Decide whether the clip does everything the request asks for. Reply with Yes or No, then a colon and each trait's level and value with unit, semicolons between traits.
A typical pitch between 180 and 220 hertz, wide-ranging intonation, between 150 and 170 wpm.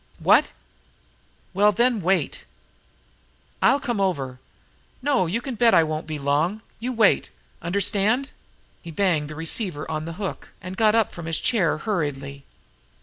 No: medium, 185 Hz; wide, 6.0 semitones; average, 140 wpm